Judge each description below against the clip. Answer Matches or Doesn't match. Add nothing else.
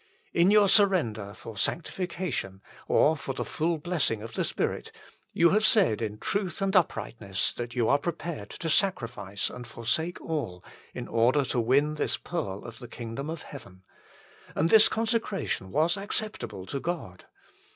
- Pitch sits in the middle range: Matches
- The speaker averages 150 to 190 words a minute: Matches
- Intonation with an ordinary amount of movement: Doesn't match